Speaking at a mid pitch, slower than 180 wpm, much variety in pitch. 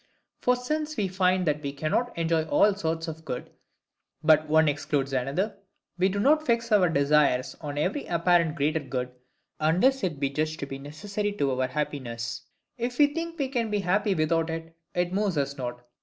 No: medium, 165 Hz; average, 185 wpm; wide, 6.1 semitones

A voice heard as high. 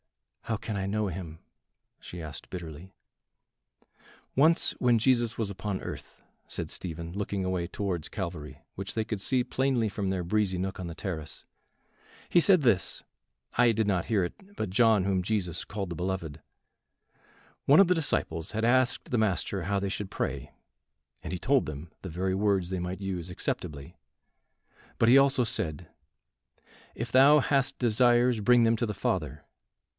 No: low, 100 Hz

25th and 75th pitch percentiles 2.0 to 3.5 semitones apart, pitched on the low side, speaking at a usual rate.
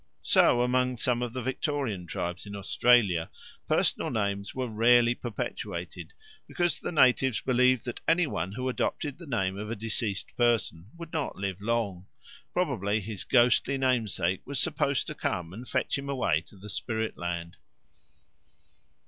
No: average, 4.4 semitones; low, 115 Hz; average, 155 wpm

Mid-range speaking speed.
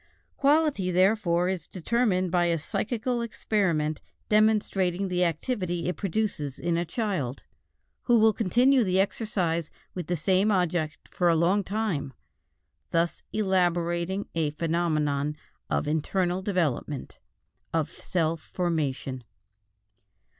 No: slow, 115 wpm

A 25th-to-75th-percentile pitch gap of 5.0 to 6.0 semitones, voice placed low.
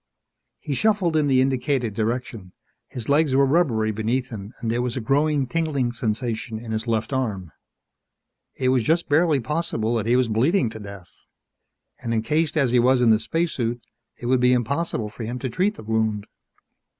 No: average, 4.1 semitones; low, 125 Hz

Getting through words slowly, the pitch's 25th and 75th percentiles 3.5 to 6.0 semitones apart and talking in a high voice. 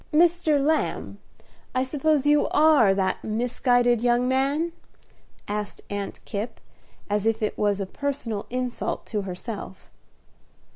Yes: slow, 125 wpm; wide, 5.4 semitones; high, 245 Hz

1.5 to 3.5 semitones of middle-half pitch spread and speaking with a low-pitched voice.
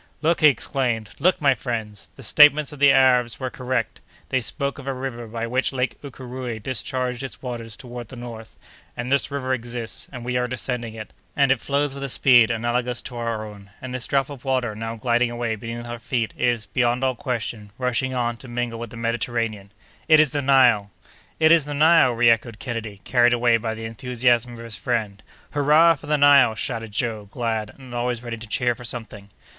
Yes: narrow, 2.4 semitones; low, 120 Hz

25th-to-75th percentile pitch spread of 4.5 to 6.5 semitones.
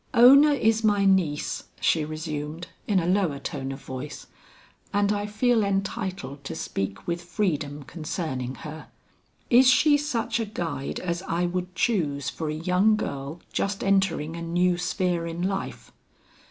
Yes: average, 5.0 semitones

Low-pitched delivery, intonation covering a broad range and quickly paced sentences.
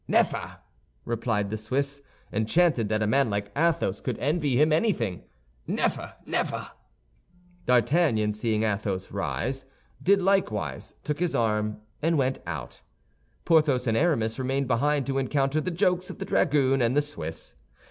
No: low, 130 Hz; wide, 5.8 semitones; average, 145 wpm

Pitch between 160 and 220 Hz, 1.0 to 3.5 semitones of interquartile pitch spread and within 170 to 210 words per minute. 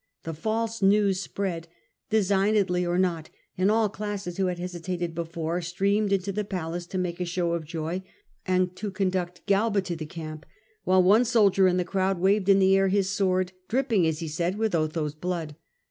Yes: medium, 185 Hz; narrow, 2.5 semitones; average, 190 wpm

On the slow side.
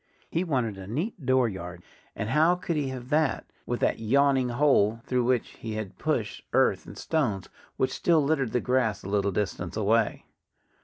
No: average, 175 wpm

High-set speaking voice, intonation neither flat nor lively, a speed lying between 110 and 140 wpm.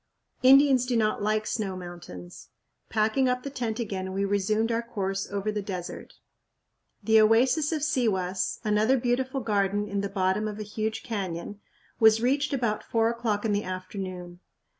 No: high, 215 Hz; average, 3.4 semitones; average, 160 wpm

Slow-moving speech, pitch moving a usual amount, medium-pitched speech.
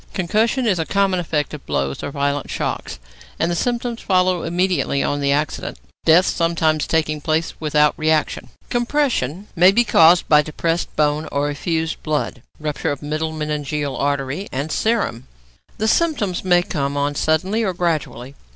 No: average, 160 wpm; average, 4.0 semitones; medium, 160 Hz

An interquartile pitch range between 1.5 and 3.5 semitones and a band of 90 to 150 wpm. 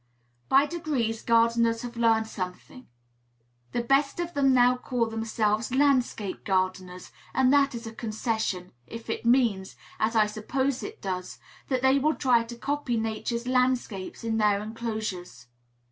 Yes: average, 3.0 semitones; average, 145 wpm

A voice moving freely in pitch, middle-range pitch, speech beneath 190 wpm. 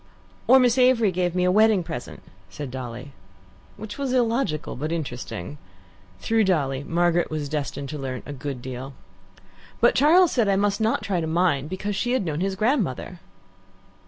Yes: wide, 7.3 semitones; medium, 175 Hz; average, 170 wpm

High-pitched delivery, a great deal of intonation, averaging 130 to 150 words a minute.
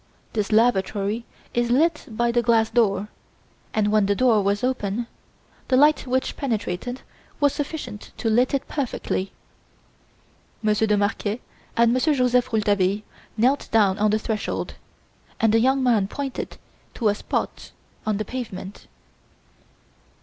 No: high, 225 Hz; average, 3.3 semitones; average, 140 wpm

